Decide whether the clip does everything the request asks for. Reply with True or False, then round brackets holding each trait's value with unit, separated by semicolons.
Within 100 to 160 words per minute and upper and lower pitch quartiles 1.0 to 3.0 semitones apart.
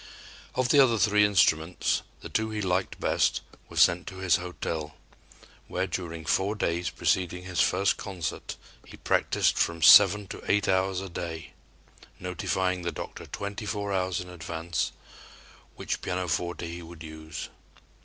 True (150 wpm; 2.7 semitones)